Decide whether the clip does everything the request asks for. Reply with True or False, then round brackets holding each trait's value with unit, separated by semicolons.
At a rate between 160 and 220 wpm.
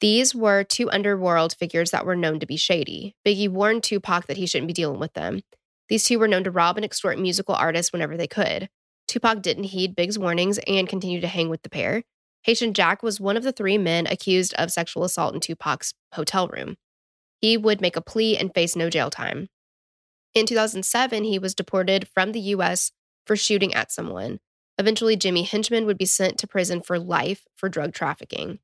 True (205 wpm)